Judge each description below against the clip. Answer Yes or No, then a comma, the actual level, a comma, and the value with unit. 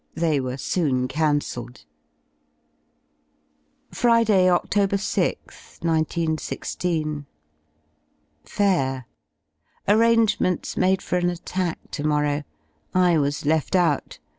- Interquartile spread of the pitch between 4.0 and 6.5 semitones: Yes, average, 4.3 semitones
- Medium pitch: Yes, medium, 165 Hz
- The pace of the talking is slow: Yes, slow, 90 wpm